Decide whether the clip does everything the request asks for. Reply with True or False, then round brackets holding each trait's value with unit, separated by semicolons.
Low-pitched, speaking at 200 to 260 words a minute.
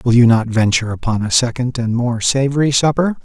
True (120 Hz; 205 wpm)